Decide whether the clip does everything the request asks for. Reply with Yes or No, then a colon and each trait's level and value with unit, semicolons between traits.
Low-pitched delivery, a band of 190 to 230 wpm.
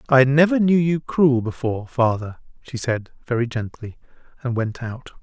No: low, 130 Hz; average, 160 wpm